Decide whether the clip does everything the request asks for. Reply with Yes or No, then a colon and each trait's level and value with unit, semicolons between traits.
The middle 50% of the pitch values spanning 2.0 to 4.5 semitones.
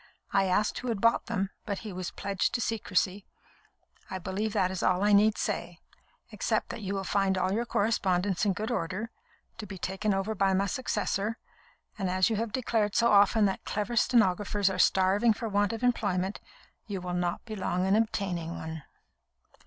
Yes: narrow, 2.5 semitones